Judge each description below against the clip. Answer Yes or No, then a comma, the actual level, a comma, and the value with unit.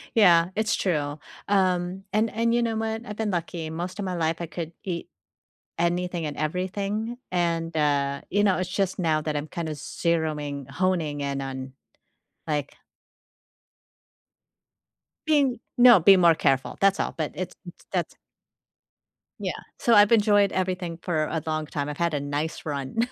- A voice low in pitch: No, medium, 170 Hz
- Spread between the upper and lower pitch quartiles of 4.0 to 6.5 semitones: Yes, average, 4.5 semitones